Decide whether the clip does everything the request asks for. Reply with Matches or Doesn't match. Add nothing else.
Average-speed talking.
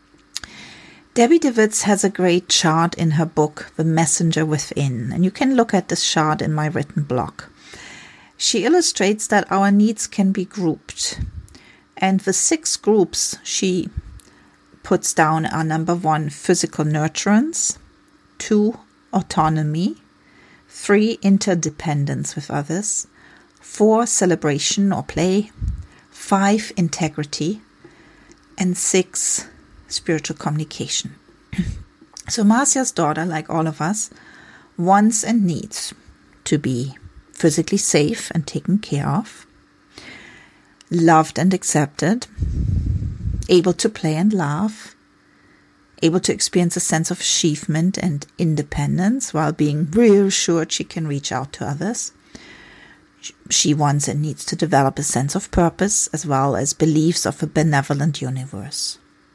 Doesn't match